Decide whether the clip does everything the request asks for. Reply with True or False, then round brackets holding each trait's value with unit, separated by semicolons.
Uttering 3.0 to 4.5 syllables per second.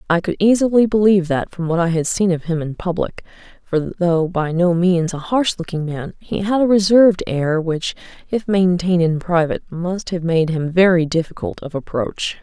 False (5.0 syllables/s)